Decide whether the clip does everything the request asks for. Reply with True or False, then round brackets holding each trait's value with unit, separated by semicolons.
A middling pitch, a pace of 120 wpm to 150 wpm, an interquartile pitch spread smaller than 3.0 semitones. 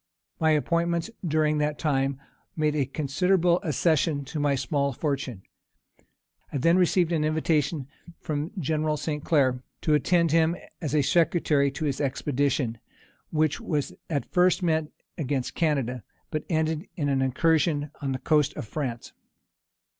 True (150 Hz; 145 wpm; 2.6 semitones)